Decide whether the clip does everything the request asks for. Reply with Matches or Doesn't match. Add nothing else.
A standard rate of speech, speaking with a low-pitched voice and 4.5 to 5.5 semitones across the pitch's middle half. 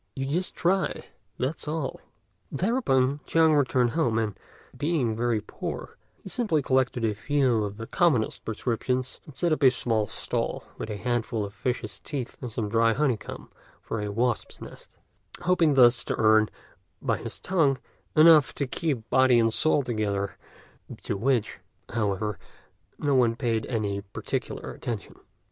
Matches